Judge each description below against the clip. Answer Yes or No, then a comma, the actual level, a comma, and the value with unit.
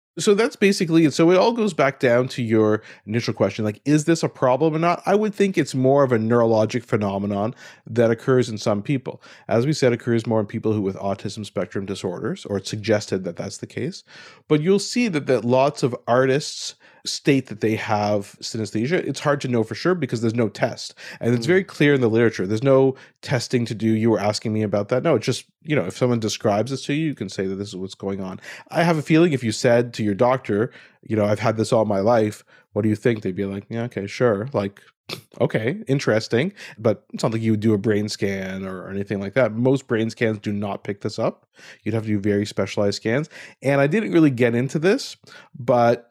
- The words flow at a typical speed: No, fast, 240 wpm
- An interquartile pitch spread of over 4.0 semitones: Yes, average, 4.8 semitones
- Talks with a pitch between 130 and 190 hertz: No, low, 115 Hz